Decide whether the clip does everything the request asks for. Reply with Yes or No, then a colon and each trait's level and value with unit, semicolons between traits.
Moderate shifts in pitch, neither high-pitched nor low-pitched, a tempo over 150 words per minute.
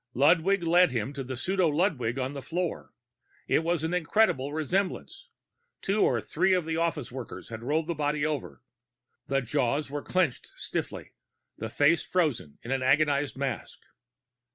Yes: average, 4.6 semitones; medium, 150 Hz; average, 160 wpm